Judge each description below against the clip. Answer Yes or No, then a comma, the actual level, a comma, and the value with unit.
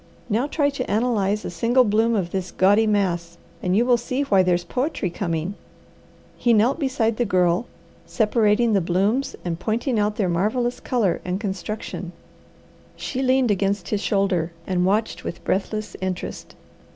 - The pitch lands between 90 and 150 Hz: No, high, 210 Hz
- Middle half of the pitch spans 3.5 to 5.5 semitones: Yes, average, 4.4 semitones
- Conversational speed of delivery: Yes, average, 160 wpm